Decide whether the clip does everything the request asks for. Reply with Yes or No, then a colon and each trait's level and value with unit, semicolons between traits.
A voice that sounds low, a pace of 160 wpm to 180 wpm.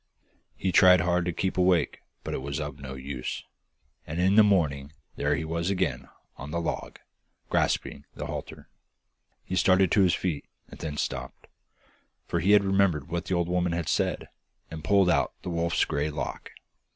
Yes: very low, 85 Hz; average, 175 wpm